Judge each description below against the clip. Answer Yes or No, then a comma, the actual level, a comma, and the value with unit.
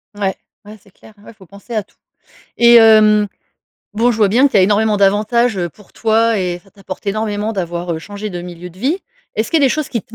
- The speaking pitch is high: Yes, high, 210 Hz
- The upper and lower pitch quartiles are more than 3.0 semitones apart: No, narrow, 2.5 semitones